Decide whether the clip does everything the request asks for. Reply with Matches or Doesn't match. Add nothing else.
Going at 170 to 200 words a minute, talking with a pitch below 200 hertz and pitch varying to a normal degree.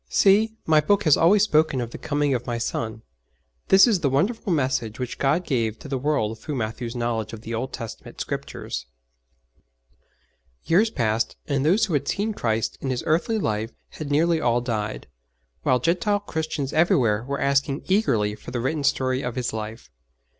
Doesn't match